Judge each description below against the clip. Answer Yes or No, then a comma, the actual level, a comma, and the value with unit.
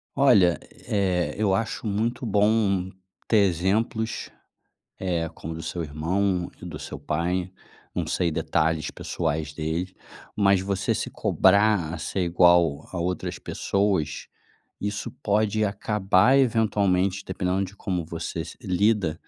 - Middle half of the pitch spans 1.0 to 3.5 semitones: Yes, average, 3.2 semitones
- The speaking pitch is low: Yes, very low, 95 Hz